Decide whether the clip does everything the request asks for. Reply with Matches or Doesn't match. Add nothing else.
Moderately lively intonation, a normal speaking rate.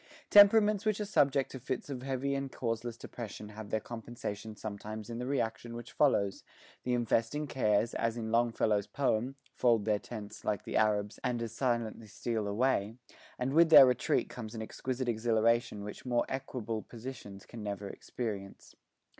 Matches